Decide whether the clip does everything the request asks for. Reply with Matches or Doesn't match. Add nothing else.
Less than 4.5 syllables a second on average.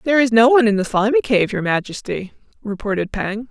Doesn't match